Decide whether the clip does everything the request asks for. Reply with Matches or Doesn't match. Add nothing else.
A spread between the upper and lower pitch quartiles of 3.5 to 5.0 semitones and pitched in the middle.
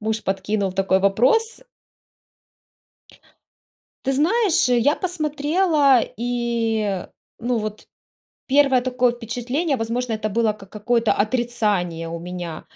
Doesn't match